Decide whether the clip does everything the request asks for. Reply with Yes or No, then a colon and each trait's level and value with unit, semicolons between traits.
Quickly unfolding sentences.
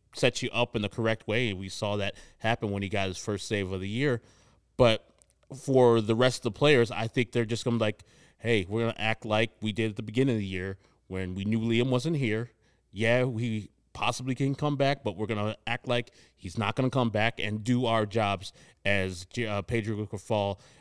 Yes: fast, 235 wpm